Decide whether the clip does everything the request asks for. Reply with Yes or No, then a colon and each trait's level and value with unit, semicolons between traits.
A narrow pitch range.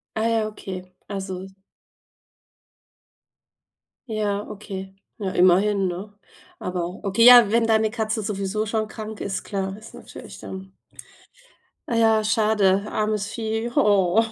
Yes: narrow, 2.3 semitones